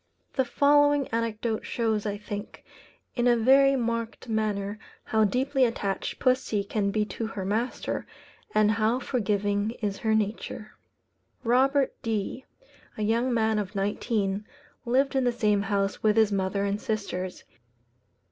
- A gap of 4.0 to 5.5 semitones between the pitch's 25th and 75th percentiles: No, average, 3.0 semitones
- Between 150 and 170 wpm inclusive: No, average, 140 wpm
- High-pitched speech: Yes, high, 220 Hz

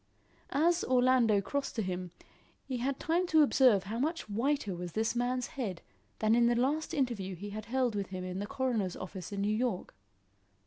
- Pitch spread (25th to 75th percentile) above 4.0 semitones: Yes, average, 4.7 semitones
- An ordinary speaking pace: Yes, average, 190 wpm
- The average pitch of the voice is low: No, high, 230 Hz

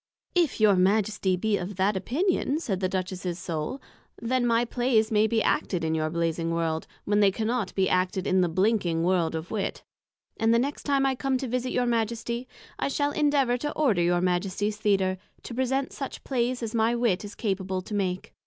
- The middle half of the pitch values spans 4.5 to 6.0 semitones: Yes, average, 4.9 semitones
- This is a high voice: Yes, high, 210 Hz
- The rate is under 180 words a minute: No, average, 200 wpm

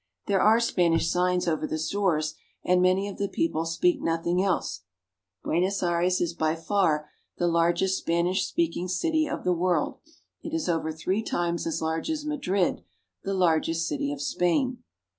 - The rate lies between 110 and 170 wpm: Yes, average, 165 wpm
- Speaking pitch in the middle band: Yes, medium, 180 Hz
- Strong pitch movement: No, average, 3.4 semitones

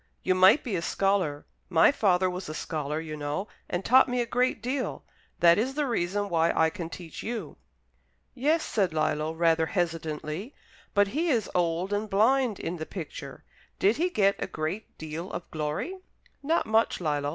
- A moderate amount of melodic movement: No, wide, 5.9 semitones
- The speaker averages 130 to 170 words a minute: No, average, 180 wpm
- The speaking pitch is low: No, medium, 185 Hz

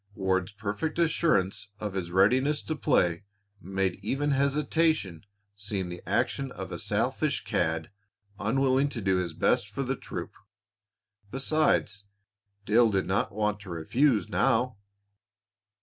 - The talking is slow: Yes, slow, 130 wpm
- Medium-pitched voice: No, low, 105 Hz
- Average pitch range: No, wide, 6.2 semitones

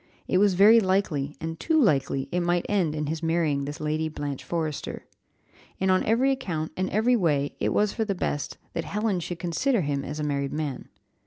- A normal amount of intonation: Yes, average, 5.0 semitones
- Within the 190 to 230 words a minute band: Yes, average, 200 wpm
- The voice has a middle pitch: Yes, medium, 165 Hz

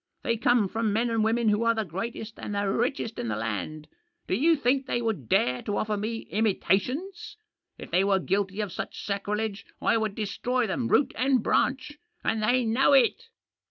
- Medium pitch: No, high, 220 Hz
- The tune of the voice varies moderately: Yes, average, 3.4 semitones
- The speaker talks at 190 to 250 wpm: Yes, average, 195 wpm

